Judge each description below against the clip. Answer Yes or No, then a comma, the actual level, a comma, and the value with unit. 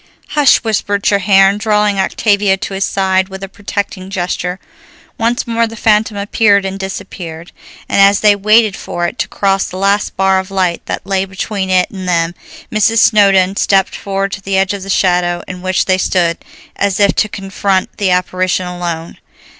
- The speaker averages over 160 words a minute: Yes, average, 180 wpm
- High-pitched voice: Yes, high, 195 Hz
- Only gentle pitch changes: Yes, narrow, 1.5 semitones